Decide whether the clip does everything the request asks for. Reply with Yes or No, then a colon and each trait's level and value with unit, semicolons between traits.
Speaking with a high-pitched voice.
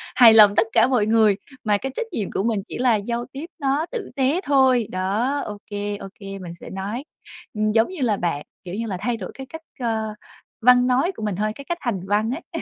Yes: high, 225 Hz